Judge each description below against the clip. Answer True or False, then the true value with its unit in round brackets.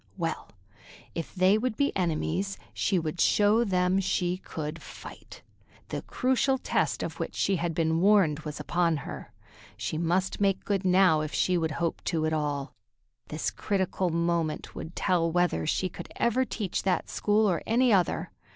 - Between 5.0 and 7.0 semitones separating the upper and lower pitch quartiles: False (3.5 semitones)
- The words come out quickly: False (170 wpm)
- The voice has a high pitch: False (180 Hz)